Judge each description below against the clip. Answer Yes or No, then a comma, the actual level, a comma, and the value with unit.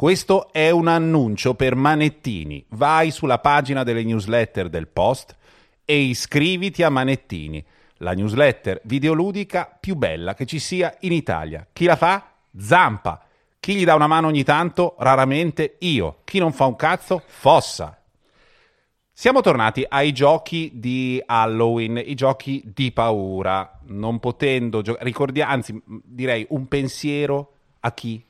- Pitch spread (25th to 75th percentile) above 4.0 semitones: Yes, wide, 5.4 semitones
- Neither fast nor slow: Yes, average, 140 wpm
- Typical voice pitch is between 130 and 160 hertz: Yes, low, 135 Hz